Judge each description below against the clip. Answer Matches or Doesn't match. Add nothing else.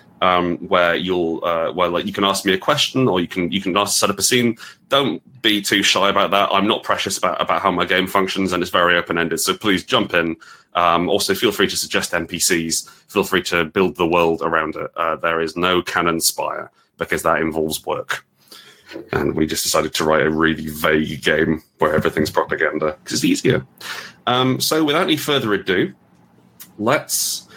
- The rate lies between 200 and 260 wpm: Matches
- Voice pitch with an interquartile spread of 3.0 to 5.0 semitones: Matches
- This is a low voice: Matches